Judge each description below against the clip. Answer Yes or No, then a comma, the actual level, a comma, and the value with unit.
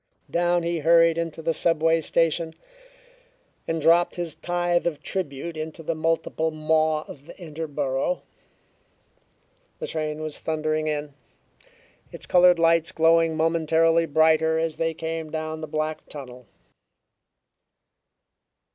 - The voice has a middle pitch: Yes, medium, 160 Hz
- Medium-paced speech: No, slow, 120 wpm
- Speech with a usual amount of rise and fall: No, narrow, 1.1 semitones